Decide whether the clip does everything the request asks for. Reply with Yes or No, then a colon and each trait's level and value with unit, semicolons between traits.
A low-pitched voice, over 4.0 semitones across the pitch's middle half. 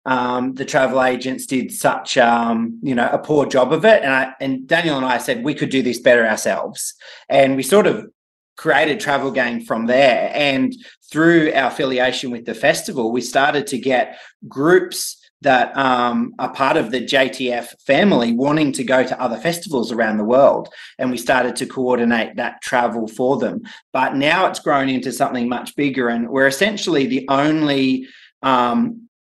No: low, 130 Hz; average, 3.1 semitones